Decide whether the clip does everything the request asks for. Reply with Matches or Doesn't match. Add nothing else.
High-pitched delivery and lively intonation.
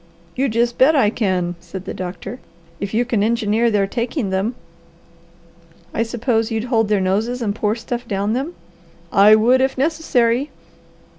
Doesn't match